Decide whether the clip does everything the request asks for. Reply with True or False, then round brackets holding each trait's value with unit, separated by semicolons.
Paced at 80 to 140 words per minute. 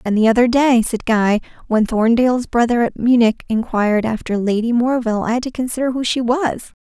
False (195 wpm)